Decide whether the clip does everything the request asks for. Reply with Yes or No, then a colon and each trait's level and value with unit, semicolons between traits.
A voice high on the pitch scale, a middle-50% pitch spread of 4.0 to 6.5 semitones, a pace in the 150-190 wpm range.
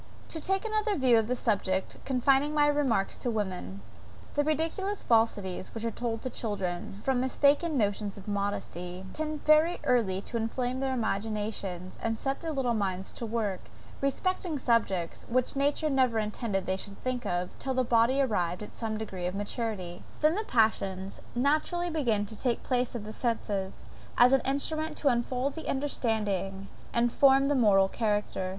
Yes: high, 235 Hz; average, 5.2 semitones; average, 170 wpm